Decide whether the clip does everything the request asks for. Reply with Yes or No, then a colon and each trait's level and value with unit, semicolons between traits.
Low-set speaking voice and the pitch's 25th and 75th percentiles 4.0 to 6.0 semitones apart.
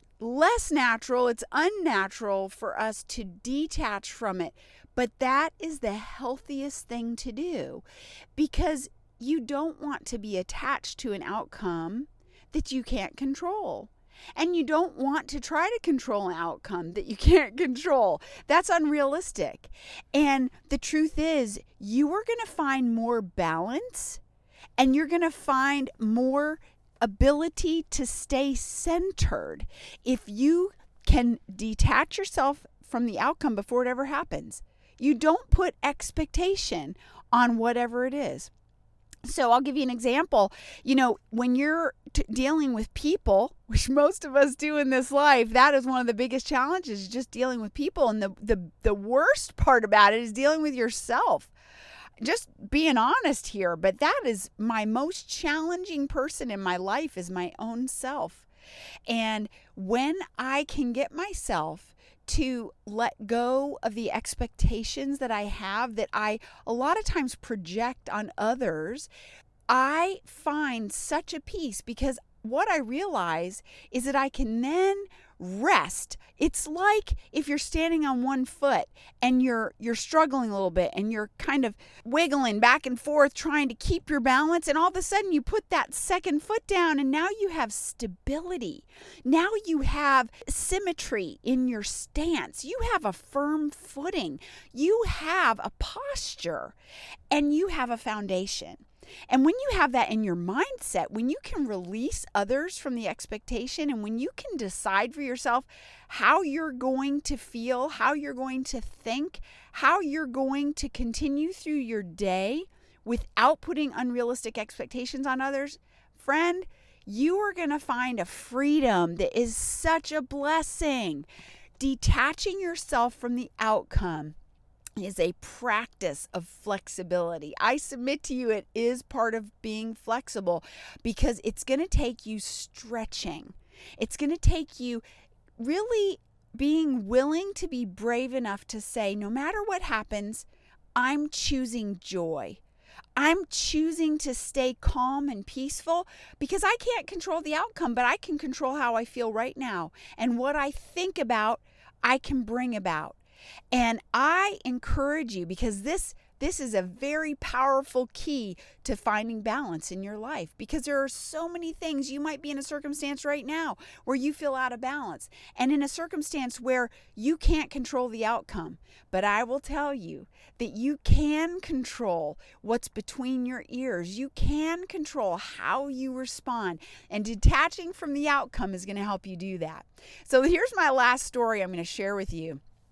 No: very high, 265 Hz; average, 5.1 semitones